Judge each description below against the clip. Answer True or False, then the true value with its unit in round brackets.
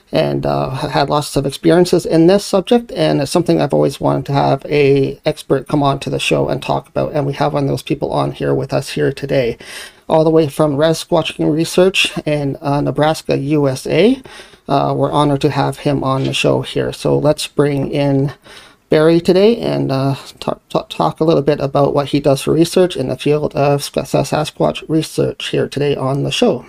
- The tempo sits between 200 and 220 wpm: True (205 wpm)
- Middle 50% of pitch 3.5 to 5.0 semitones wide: False (2.6 semitones)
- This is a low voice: False (145 Hz)